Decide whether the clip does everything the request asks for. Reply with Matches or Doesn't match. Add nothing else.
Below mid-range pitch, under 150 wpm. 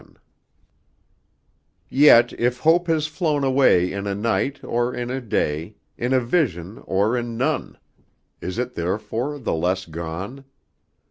Matches